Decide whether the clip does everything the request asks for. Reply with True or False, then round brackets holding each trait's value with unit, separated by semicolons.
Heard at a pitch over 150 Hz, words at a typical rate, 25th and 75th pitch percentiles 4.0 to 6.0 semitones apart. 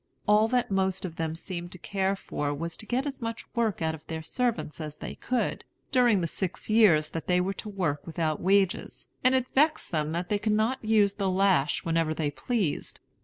False (190 Hz; 215 wpm; 5.2 semitones)